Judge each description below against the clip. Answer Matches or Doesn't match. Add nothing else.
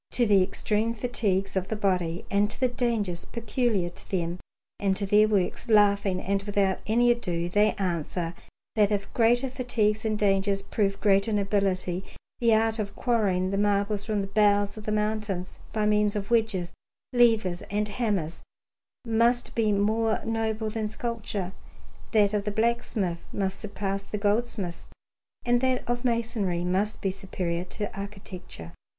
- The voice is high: Matches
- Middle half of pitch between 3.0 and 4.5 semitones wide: Doesn't match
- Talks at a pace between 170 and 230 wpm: Doesn't match